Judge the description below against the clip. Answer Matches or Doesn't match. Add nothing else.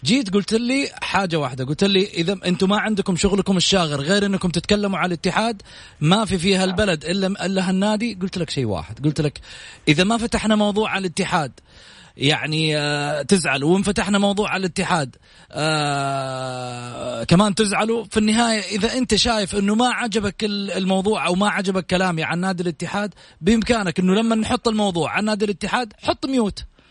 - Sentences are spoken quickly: Matches